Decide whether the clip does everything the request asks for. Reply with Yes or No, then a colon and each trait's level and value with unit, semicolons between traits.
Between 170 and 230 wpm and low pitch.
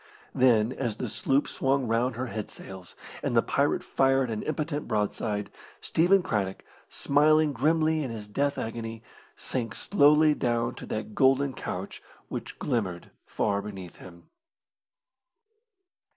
No: slow, 135 wpm; low, 120 Hz